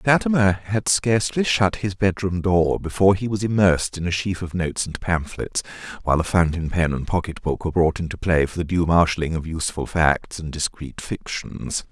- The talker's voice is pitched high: No, very low, 90 Hz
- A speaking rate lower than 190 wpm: No, average, 195 wpm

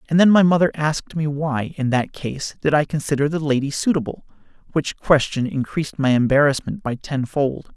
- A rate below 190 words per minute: Yes, average, 170 wpm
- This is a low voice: No, medium, 145 Hz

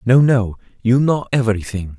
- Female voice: No, male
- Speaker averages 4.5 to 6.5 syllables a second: Yes, 5.0 syllables/s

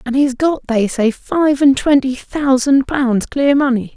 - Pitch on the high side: Yes, very high, 265 Hz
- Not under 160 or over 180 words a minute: No, average, 195 wpm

